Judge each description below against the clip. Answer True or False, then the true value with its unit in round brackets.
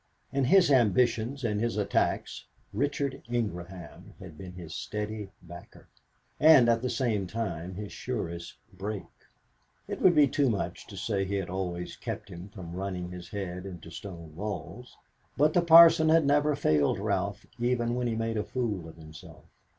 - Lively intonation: True (5.9 semitones)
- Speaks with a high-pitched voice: False (105 Hz)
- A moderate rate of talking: True (170 wpm)